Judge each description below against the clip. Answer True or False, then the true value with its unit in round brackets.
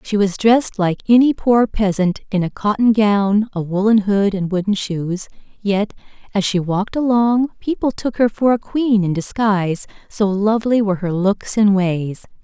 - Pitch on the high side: True (205 Hz)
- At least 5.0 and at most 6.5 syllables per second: False (4.7 syllables/s)